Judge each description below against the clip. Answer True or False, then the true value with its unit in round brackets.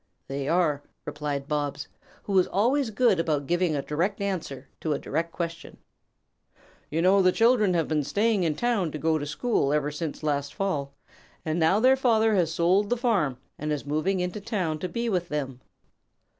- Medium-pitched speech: True (170 Hz)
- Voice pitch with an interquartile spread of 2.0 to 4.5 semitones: False (5.1 semitones)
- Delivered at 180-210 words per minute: True (185 wpm)